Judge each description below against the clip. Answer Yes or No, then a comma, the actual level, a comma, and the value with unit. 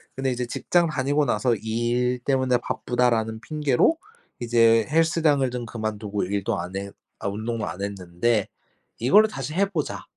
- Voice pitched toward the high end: No, low, 120 Hz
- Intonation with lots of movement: No, average, 4.1 semitones